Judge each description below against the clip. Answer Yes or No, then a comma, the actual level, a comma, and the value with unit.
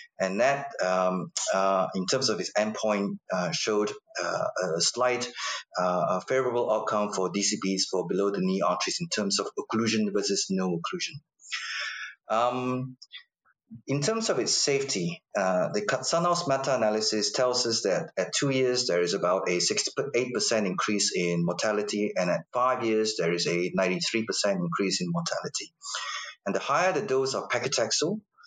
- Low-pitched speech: Yes, low, 110 Hz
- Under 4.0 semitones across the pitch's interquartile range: No, average, 5.3 semitones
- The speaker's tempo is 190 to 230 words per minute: No, average, 155 wpm